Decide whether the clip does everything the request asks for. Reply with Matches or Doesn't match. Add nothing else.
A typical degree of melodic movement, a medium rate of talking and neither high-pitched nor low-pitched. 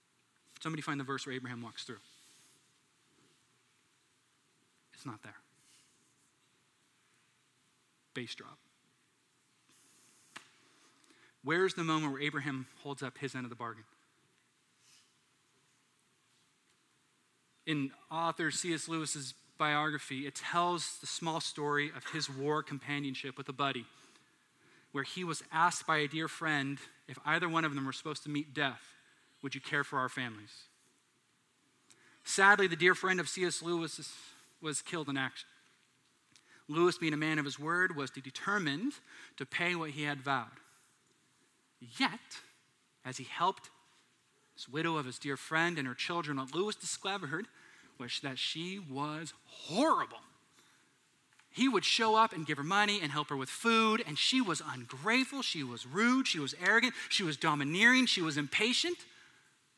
Matches